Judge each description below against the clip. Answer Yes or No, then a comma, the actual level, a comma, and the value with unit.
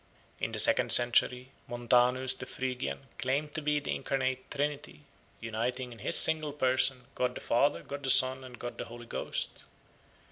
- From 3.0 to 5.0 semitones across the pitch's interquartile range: No, narrow, 2.4 semitones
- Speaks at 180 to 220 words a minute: No, average, 170 wpm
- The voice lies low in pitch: Yes, low, 130 Hz